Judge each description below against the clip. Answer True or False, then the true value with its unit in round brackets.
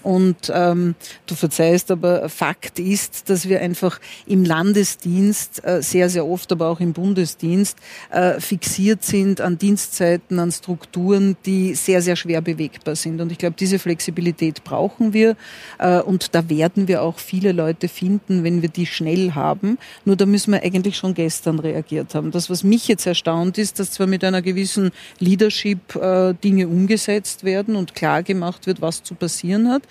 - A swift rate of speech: False (175 wpm)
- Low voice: False (180 Hz)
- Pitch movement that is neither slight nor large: False (2.3 semitones)